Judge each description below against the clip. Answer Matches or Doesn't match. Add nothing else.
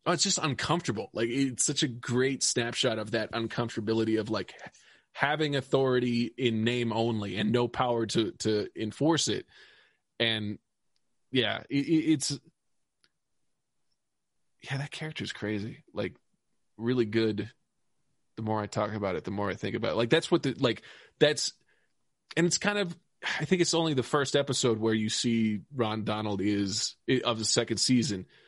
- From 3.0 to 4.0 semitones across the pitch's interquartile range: Doesn't match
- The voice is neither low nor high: Doesn't match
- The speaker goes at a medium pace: Matches